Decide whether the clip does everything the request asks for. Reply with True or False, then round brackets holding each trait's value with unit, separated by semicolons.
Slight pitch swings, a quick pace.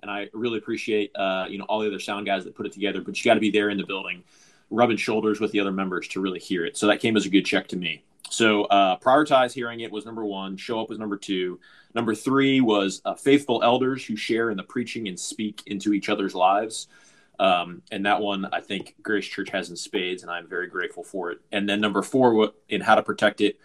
True (2.3 semitones; 255 wpm)